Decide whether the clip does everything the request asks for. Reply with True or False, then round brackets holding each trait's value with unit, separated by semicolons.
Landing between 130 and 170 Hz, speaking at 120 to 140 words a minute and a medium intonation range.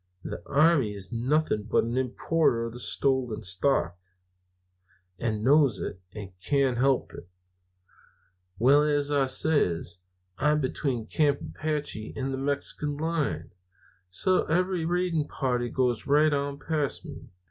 True (135 Hz; 135 wpm; 4.5 semitones)